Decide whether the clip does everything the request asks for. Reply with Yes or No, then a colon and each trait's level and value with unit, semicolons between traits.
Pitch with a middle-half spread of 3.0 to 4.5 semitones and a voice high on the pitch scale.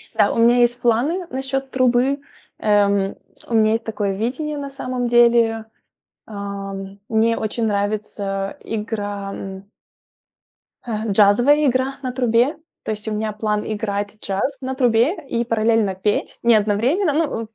Yes: average, 3.5 semitones; high, 225 Hz